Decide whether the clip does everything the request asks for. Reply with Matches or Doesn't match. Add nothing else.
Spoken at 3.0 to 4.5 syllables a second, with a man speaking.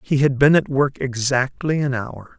Matches